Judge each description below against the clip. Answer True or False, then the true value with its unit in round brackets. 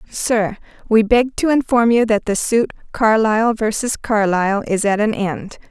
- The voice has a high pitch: True (220 Hz)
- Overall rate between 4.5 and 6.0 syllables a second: False (4.3 syllables/s)